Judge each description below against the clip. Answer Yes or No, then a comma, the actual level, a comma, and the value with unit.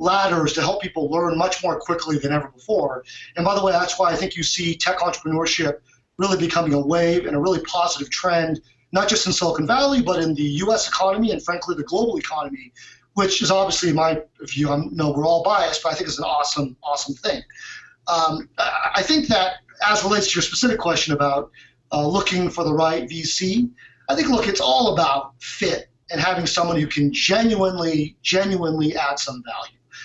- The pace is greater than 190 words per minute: Yes, average, 200 wpm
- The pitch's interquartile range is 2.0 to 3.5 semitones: No, average, 4.0 semitones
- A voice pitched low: No, medium, 170 Hz